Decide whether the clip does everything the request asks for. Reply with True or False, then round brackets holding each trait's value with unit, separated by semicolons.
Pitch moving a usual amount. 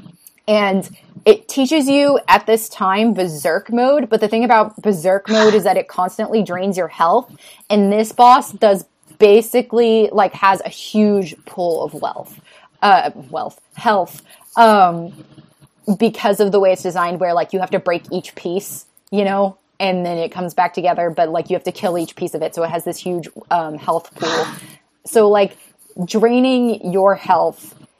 True (3.5 semitones)